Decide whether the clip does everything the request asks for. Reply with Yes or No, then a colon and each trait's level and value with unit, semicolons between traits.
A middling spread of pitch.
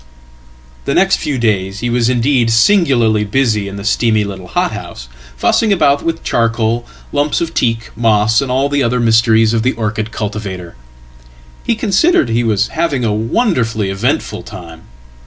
Yes: average, 3.9 semitones